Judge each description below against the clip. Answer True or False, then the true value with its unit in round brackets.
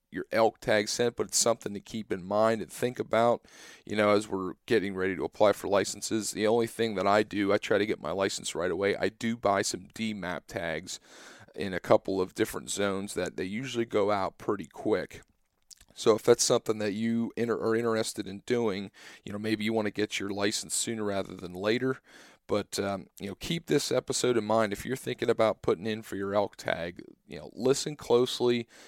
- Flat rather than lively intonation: True (2.3 semitones)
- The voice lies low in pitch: True (110 Hz)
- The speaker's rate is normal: False (220 wpm)